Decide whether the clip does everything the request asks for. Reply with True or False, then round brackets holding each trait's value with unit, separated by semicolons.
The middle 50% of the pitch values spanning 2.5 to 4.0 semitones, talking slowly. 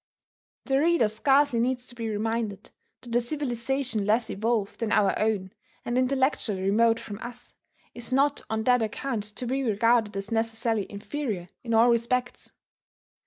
False (2.8 semitones; 155 wpm)